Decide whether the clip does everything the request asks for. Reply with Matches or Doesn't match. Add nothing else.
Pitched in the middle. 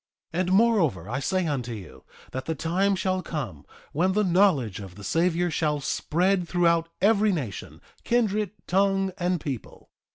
Matches